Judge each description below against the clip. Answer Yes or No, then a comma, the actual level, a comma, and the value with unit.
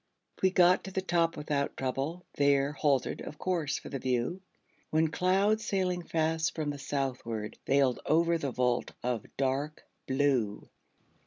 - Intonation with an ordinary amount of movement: Yes, average, 4.2 semitones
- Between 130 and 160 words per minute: Yes, average, 150 wpm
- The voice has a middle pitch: Yes, medium, 145 Hz